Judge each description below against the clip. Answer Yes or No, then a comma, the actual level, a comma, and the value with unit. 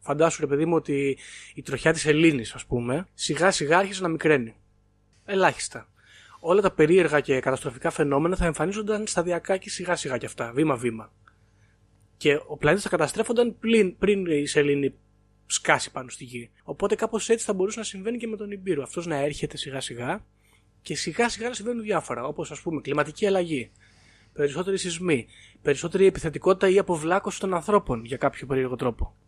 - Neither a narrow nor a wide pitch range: No, wide, 6.9 semitones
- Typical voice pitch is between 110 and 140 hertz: No, medium, 150 Hz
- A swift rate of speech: Yes, fast, 175 wpm